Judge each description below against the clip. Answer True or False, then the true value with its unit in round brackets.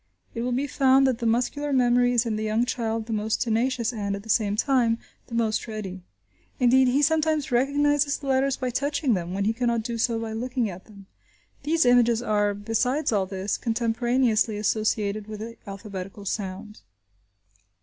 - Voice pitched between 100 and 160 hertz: False (230 Hz)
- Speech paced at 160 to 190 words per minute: True (180 wpm)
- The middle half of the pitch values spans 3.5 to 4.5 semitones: False (3.0 semitones)